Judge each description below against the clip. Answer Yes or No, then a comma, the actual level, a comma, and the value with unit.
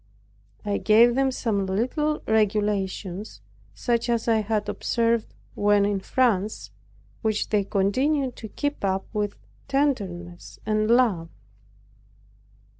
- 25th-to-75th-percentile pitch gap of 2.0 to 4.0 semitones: Yes, average, 3.2 semitones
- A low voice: No, high, 215 Hz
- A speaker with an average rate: No, slow, 115 wpm